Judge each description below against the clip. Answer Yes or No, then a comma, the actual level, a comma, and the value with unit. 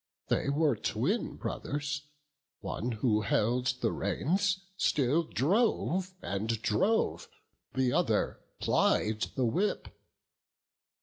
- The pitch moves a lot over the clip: Yes, wide, 8.1 semitones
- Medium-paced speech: No, slow, 100 wpm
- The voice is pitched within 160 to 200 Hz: No, medium, 140 Hz